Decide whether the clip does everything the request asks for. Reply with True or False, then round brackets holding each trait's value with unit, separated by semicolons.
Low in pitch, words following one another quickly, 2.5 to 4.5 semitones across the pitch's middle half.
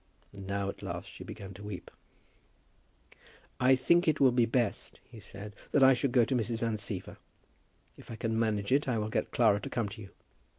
True (115 Hz; 210 wpm; 3.7 semitones)